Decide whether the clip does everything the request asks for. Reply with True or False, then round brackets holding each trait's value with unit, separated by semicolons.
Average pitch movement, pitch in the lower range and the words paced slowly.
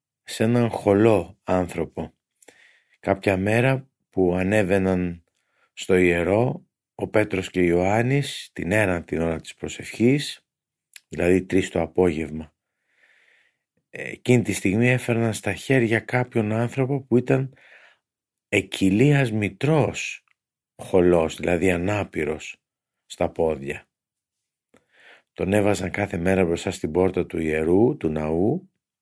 True (4.6 semitones; 95 Hz; 110 wpm)